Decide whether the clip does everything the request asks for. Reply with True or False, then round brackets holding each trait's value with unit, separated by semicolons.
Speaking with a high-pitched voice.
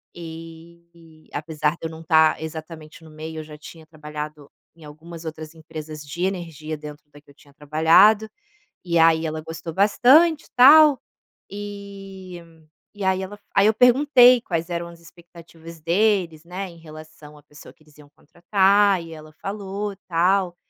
False (165 Hz)